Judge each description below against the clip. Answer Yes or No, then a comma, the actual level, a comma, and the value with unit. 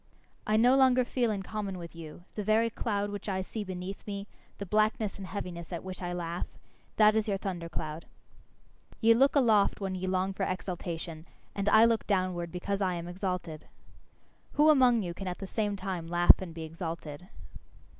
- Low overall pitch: No, high, 190 Hz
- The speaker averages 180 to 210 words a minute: Yes, average, 190 wpm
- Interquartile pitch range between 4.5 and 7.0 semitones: No, average, 3.5 semitones